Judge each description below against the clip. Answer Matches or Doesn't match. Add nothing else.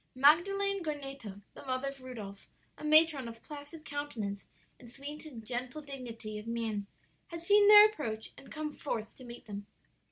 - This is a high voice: Matches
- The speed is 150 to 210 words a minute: Matches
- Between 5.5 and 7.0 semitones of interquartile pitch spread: Doesn't match